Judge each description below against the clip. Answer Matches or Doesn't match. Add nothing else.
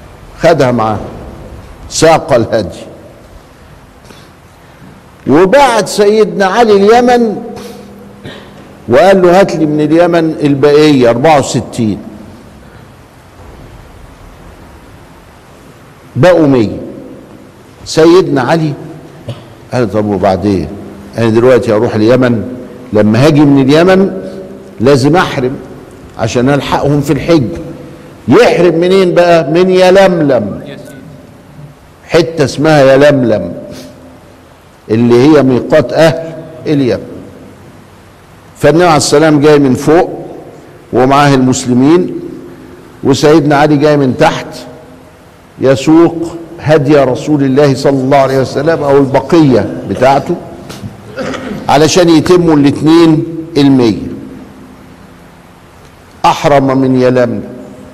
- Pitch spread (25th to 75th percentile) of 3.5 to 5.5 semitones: Matches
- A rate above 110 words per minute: Doesn't match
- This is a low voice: Doesn't match